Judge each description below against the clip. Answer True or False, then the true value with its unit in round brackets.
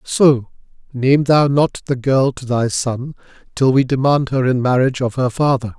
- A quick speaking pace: False (185 wpm)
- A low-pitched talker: True (130 Hz)